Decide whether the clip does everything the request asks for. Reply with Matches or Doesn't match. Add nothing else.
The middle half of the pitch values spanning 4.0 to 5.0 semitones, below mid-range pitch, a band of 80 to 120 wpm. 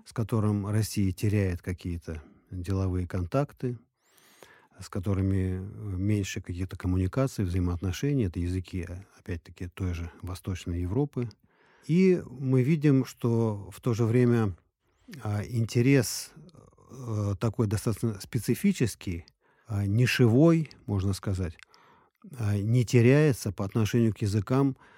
Matches